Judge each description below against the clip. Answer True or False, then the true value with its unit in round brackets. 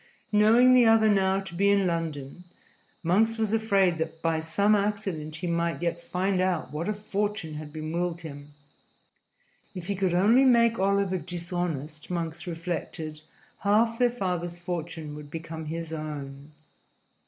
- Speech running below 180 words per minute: True (155 wpm)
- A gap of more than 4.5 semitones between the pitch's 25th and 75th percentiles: False (3.9 semitones)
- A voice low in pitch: False (175 Hz)